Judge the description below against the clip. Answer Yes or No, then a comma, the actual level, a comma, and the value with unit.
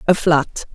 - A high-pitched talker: No, medium, 160 Hz